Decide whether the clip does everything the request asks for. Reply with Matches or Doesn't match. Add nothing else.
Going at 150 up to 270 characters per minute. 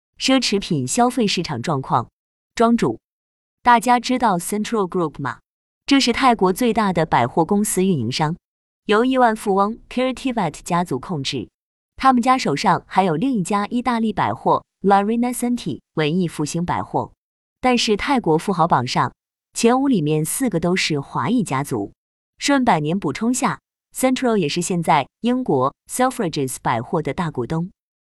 Doesn't match